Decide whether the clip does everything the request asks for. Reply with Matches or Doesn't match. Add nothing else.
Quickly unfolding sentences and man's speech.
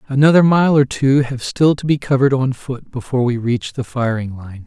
Matches